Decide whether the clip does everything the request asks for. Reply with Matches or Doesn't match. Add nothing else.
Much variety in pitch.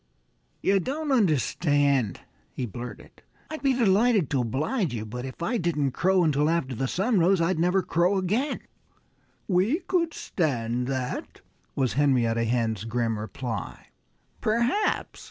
Matches